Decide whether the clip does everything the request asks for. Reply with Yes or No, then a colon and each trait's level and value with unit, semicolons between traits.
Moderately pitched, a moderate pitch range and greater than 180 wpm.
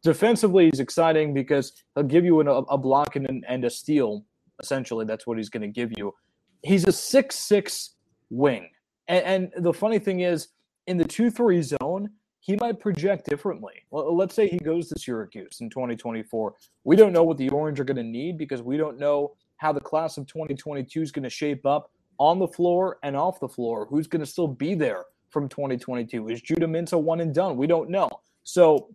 Yes: medium, 155 Hz; average, 4.7 semitones; fast, 205 wpm